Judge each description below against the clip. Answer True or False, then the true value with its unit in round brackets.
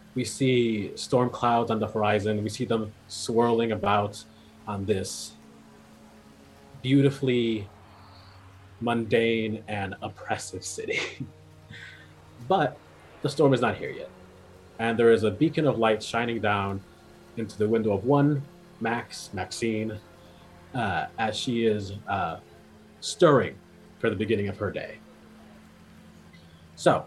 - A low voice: True (110 Hz)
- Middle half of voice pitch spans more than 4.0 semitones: False (2.9 semitones)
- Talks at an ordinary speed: False (120 wpm)